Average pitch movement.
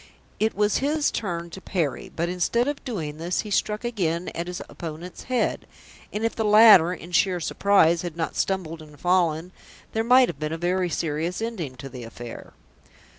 Yes: average, 4.5 semitones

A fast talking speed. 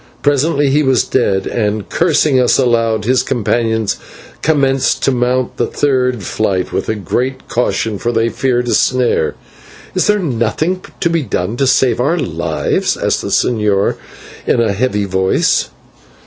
No: average, 150 wpm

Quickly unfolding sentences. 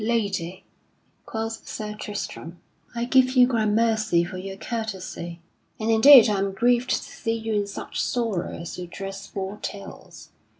No: average, 145 wpm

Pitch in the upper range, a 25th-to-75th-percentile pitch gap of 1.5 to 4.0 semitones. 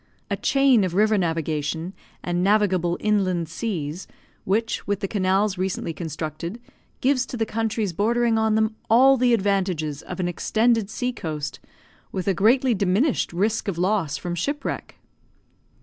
No: high, 200 Hz; average, 4.4 semitones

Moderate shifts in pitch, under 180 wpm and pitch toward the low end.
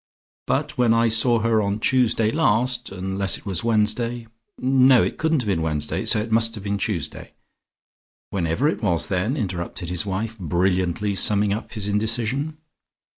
Yes: average, 3.4 semitones; average, 170 wpm; low, 110 Hz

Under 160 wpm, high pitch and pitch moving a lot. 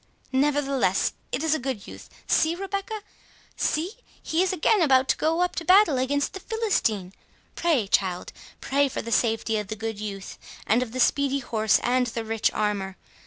No: average, 165 wpm; very high, 265 Hz; wide, 6.5 semitones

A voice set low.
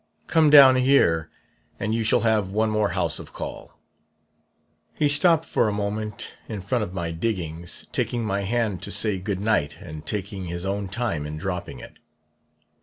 Yes: low, 100 Hz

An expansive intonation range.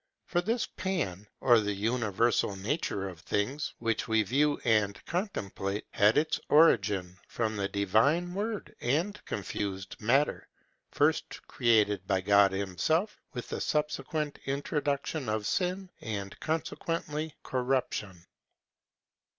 Yes: wide, 7.1 semitones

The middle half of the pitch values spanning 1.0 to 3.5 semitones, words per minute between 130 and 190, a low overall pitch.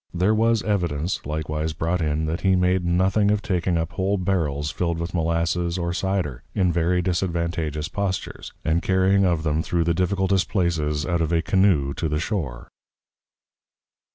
Yes: average, 2.9 semitones; average, 165 wpm; very low, 85 Hz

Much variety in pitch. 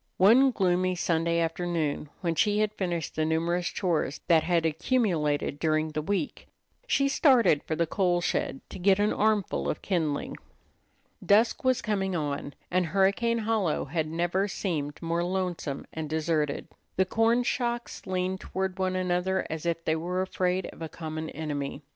No: average, 3.5 semitones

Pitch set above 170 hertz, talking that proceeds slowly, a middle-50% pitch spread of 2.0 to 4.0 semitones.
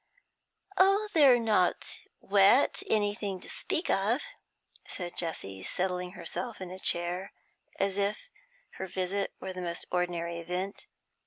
Yes: high, 190 Hz; slow, 130 wpm; narrow, 2.6 semitones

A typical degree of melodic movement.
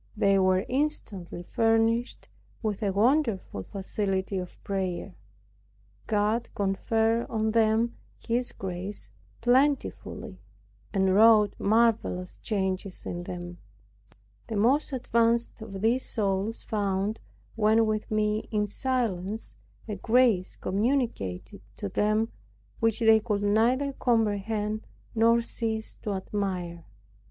Yes: average, 3.0 semitones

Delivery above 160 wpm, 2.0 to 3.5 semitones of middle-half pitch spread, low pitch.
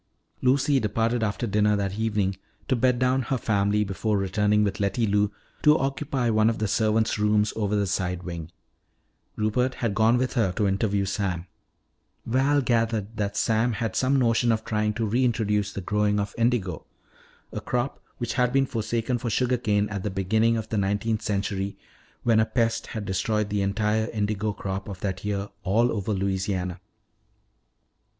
Yes: average, 170 wpm; narrow, 2.6 semitones; low, 105 Hz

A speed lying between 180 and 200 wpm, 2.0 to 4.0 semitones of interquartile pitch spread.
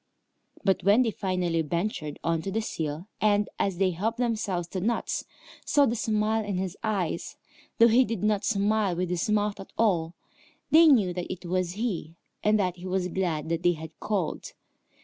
Yes: average, 190 wpm; average, 3.6 semitones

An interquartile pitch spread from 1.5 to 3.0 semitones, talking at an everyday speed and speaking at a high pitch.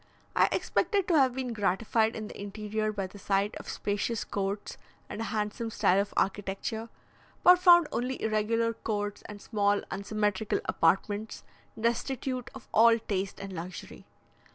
Yes: narrow, 2.4 semitones; average, 150 wpm; high, 215 Hz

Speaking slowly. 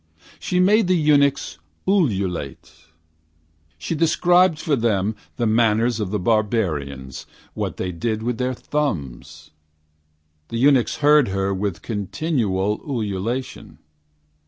Yes: slow, 110 wpm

